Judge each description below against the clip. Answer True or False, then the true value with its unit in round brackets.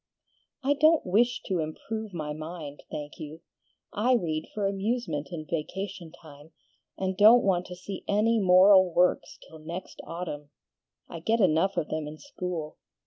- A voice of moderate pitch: True (180 Hz)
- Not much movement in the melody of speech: False (4.6 semitones)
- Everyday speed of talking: True (155 wpm)